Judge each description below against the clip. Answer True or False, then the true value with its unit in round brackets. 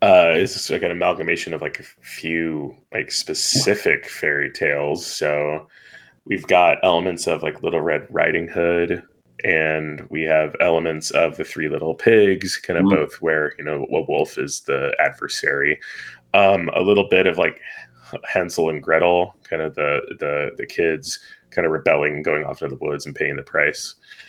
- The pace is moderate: True (175 wpm)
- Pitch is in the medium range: False (100 Hz)